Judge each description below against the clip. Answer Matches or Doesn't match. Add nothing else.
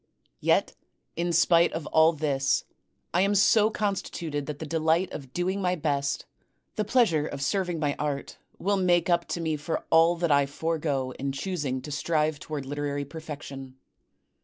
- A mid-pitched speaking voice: Matches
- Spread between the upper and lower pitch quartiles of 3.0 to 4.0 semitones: Matches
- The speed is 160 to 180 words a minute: Matches